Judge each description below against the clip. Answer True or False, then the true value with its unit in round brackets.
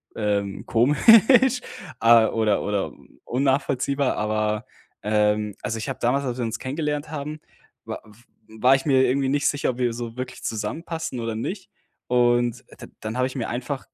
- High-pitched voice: False (125 Hz)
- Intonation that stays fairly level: False (3.9 semitones)